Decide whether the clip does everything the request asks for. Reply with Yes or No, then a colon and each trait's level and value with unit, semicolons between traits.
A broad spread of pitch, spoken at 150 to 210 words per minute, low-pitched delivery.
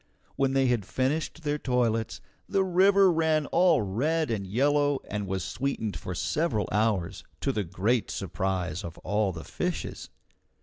Yes: wide, 7.2 semitones; average, 155 wpm; low, 120 Hz